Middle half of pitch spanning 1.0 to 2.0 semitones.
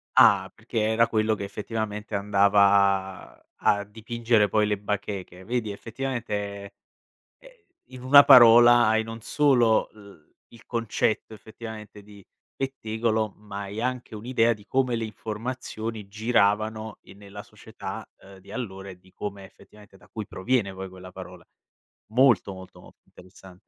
No: narrow, 2.5 semitones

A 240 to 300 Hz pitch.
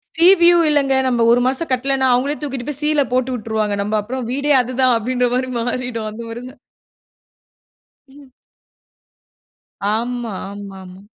Yes: very high, 250 Hz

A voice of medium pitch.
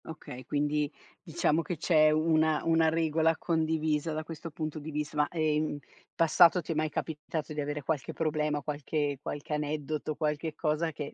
Yes: medium, 155 Hz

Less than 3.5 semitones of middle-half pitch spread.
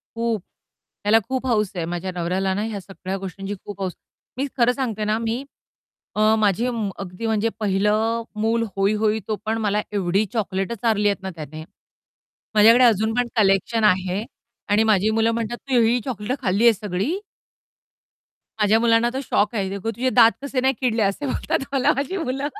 Yes: average, 3.1 semitones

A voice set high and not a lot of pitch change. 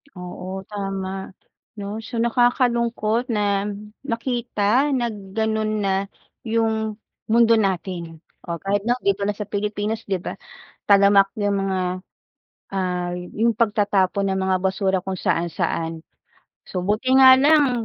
No: high, 205 Hz; average, 3.2 semitones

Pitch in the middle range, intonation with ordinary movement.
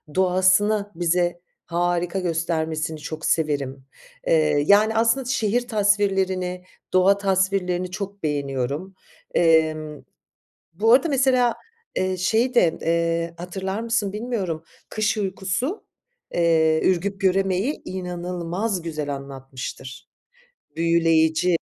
Yes: medium, 180 Hz; average, 3.7 semitones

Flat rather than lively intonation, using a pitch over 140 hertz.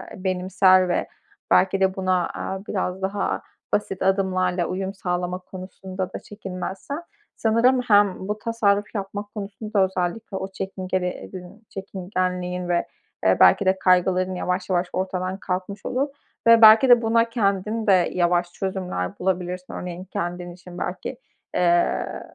Yes: narrow, 1.8 semitones; high, 190 Hz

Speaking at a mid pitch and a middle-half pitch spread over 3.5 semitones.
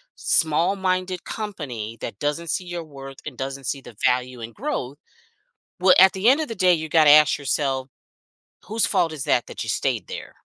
Yes: medium, 155 Hz; wide, 5.4 semitones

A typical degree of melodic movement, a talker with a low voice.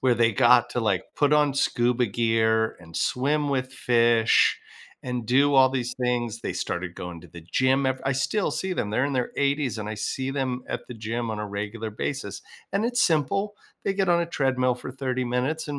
Yes: average, 3.5 semitones; low, 125 Hz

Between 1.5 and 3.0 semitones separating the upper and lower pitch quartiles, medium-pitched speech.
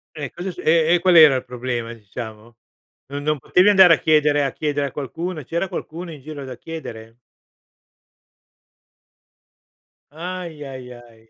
No: average, 5.0 semitones; medium, 145 Hz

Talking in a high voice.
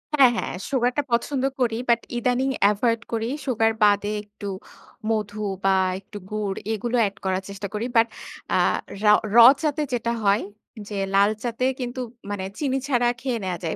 Yes: high, 225 Hz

